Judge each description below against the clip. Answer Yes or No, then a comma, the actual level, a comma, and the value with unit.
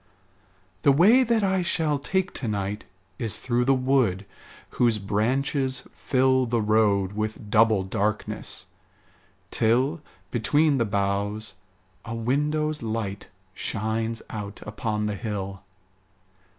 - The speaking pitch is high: No, low, 115 Hz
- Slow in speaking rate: Yes, slow, 115 wpm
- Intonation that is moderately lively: Yes, average, 4.6 semitones